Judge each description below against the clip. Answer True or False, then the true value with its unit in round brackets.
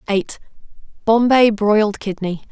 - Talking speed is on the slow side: True (70 wpm)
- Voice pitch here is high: True (210 Hz)